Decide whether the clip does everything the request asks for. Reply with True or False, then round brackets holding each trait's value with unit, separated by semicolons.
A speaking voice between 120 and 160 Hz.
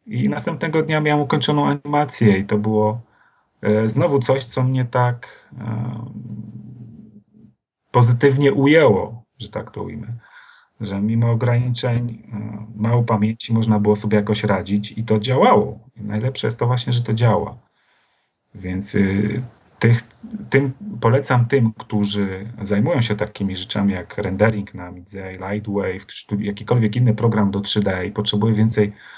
False (110 Hz)